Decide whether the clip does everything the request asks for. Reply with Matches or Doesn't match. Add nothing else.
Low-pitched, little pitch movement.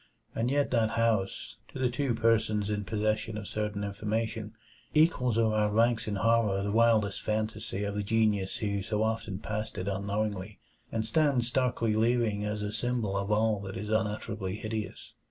Matches